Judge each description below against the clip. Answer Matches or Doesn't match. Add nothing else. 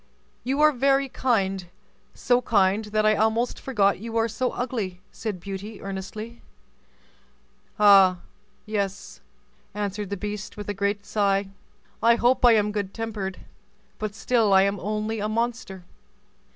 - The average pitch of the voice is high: Matches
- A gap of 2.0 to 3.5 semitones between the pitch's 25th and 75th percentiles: Matches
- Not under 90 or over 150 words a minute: Matches